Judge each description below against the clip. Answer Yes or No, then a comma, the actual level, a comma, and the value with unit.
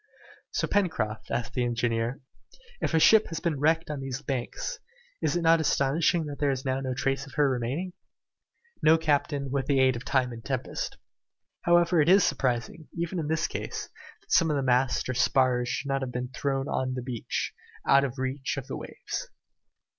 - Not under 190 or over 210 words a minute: Yes, average, 200 wpm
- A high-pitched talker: No, low, 135 Hz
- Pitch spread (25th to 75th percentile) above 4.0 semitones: No, average, 3.7 semitones